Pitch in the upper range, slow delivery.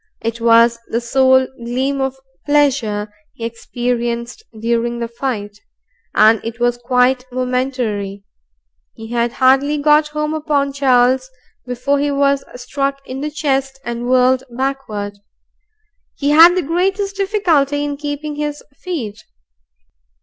Yes: very high, 260 Hz; slow, 130 wpm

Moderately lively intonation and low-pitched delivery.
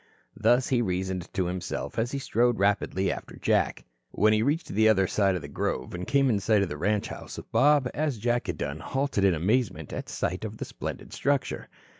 Yes: average, 4.9 semitones; low, 105 Hz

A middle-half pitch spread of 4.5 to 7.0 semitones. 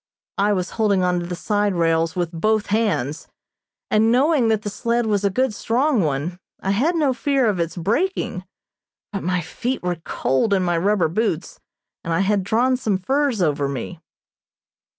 Yes: average, 5.0 semitones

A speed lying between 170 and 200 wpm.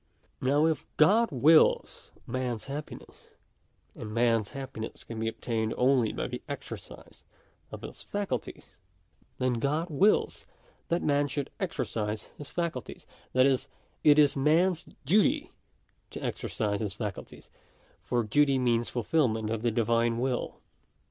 No: slow, 135 wpm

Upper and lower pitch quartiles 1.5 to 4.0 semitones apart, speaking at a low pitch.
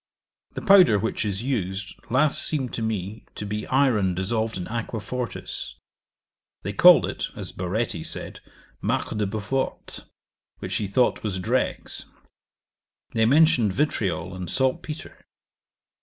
No: average, 5.0 semitones; low, 110 Hz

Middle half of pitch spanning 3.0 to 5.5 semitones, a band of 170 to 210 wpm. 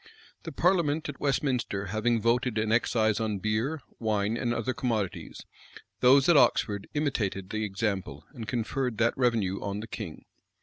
No: average, 3.4 semitones; average, 150 wpm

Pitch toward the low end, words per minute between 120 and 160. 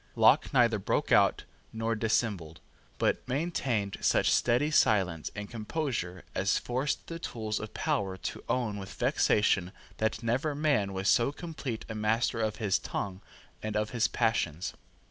Yes: low, 110 Hz; average, 150 wpm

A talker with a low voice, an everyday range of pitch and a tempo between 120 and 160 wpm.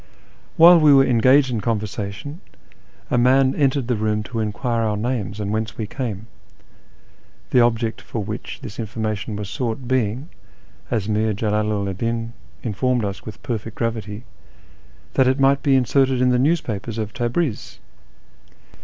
Yes: low, 115 Hz; average, 3.4 semitones; average, 155 wpm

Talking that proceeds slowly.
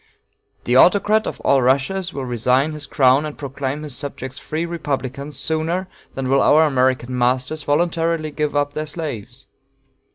No: average, 160 wpm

